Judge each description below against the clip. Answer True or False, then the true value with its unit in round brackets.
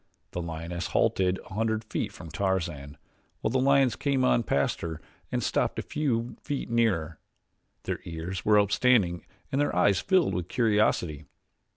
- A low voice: True (100 Hz)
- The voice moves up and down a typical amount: False (5.8 semitones)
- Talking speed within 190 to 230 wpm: False (160 wpm)